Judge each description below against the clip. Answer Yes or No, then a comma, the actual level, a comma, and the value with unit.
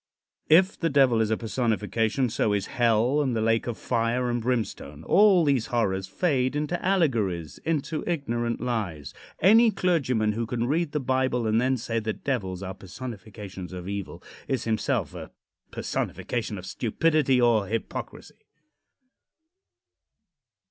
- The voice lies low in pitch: Yes, low, 120 Hz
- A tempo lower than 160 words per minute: Yes, average, 140 wpm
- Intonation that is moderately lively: Yes, average, 4.3 semitones